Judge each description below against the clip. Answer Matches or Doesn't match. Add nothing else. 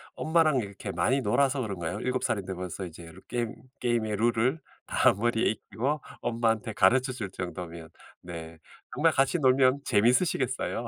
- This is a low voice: Matches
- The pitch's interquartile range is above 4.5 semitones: Matches